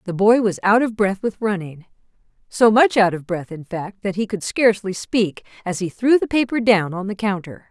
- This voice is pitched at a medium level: No, high, 205 Hz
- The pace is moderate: No, fast, 225 wpm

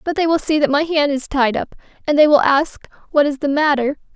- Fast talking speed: Yes, fast, 260 wpm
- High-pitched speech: Yes, very high, 290 Hz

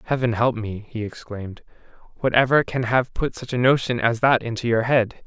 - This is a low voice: Yes, low, 120 Hz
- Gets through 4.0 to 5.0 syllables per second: No, 5.2 syllables/s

